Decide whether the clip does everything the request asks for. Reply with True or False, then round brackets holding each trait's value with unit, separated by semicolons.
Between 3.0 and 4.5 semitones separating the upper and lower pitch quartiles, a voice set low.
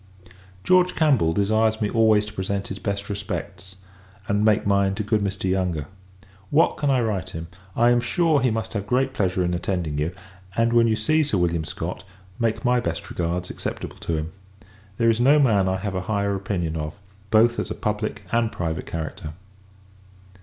True (4.0 semitones; 105 Hz)